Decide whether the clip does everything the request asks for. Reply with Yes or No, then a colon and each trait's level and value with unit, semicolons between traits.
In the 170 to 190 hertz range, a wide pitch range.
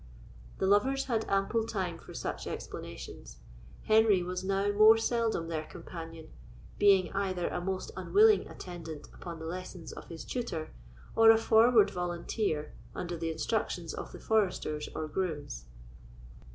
No: medium, 185 Hz; average, 4.8 semitones